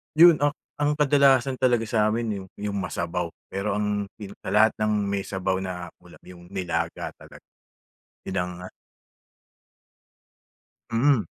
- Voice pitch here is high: No, low, 105 Hz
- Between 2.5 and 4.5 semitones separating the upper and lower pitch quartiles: No, average, 5.3 semitones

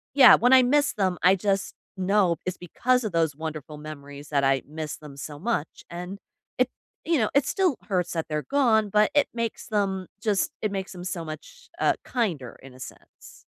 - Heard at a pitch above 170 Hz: Yes, medium, 185 Hz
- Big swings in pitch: Yes, wide, 6.6 semitones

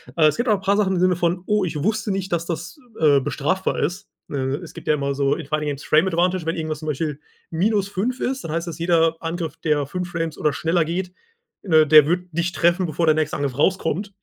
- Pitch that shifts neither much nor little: Yes, average, 3.2 semitones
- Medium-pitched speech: Yes, medium, 170 Hz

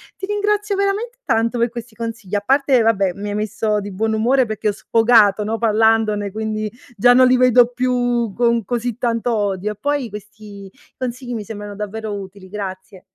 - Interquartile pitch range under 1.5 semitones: No, average, 2.8 semitones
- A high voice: Yes, high, 225 Hz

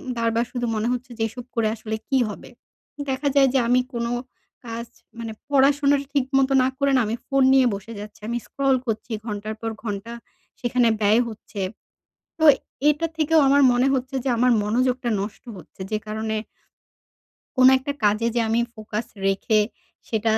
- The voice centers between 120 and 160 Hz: No, high, 235 Hz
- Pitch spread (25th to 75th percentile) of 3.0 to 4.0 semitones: Yes, average, 3.4 semitones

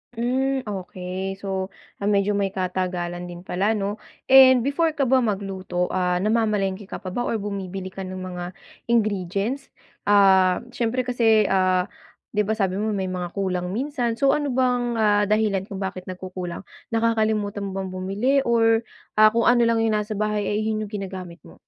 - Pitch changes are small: No, average, 3.4 semitones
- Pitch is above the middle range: Yes, high, 205 Hz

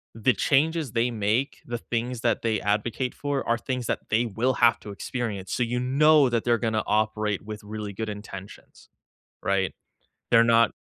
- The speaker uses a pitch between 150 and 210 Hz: No, low, 115 Hz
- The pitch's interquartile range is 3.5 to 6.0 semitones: No, average, 2.7 semitones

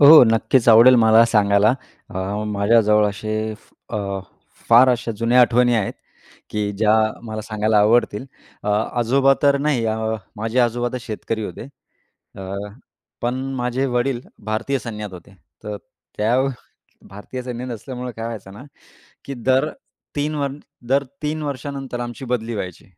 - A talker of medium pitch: No, low, 115 Hz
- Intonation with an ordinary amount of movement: Yes, average, 3.1 semitones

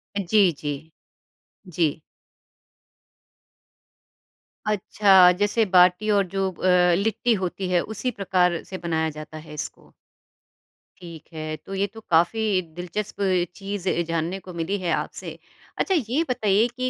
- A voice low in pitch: No, medium, 185 Hz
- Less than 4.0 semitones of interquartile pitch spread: Yes, average, 3.2 semitones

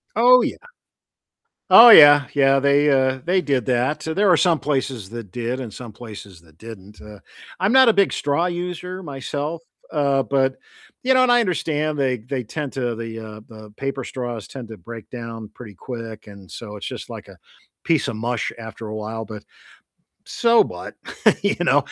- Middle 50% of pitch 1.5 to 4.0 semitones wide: No, wide, 5.4 semitones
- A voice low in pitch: Yes, low, 130 Hz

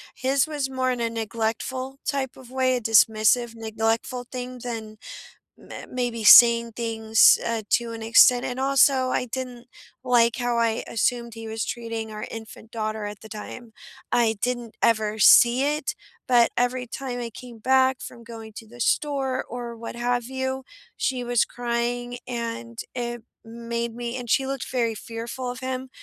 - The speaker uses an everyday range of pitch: No, narrow, 1.9 semitones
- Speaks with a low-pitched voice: No, high, 240 Hz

